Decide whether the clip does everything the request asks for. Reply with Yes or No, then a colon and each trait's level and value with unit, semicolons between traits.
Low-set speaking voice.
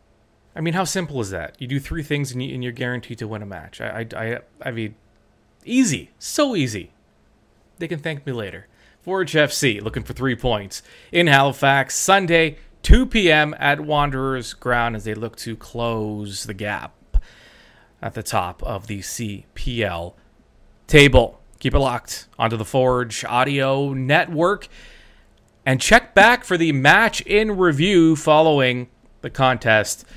Yes: low, 130 Hz